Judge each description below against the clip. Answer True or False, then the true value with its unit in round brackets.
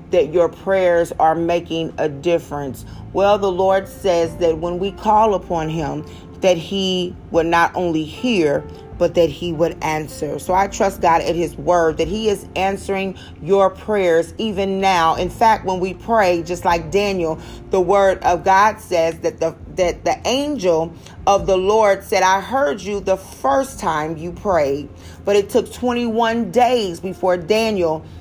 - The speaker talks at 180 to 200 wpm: False (170 wpm)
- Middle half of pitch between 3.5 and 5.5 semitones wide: False (3.0 semitones)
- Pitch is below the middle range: False (185 Hz)